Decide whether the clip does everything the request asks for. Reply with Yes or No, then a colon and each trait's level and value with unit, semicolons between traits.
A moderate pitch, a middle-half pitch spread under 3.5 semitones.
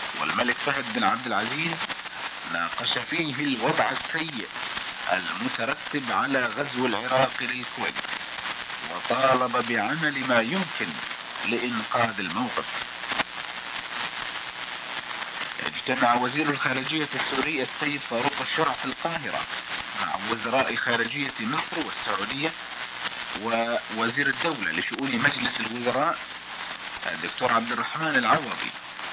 No: low, 130 Hz; average, 2.7 semitones